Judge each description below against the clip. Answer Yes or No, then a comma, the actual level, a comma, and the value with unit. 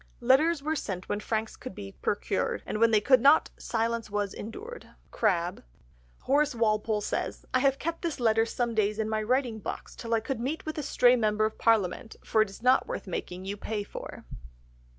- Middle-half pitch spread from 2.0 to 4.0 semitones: Yes, average, 3.5 semitones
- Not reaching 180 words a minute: No, average, 200 wpm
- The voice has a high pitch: Yes, high, 225 Hz